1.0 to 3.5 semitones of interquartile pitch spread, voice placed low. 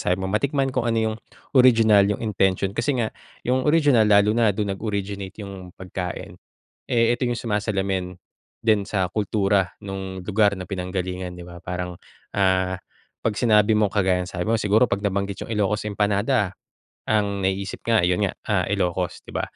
Yes: average, 2.7 semitones; low, 100 Hz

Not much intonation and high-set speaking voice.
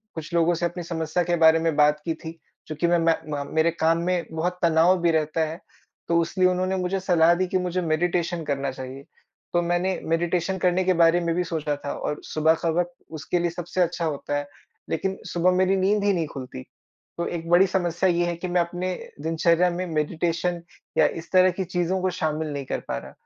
No: narrow, 1.9 semitones; medium, 170 Hz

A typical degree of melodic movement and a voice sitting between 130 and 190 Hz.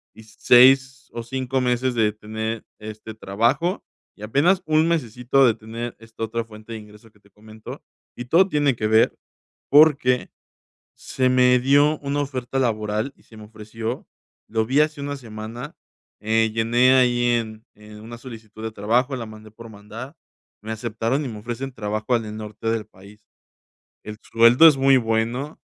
No: average, 3.3 semitones; low, 115 Hz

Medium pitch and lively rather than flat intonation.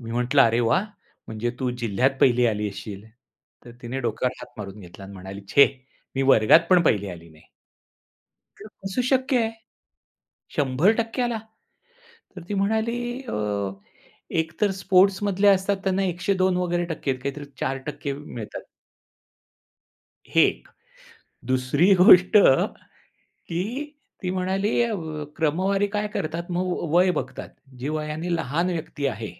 Yes: medium, 160 Hz; wide, 7.6 semitones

